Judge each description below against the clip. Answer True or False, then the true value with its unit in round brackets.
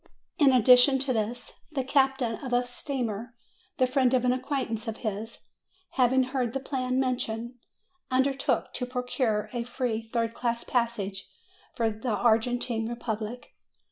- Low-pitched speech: False (245 Hz)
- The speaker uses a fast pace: False (145 wpm)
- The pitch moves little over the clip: True (2.2 semitones)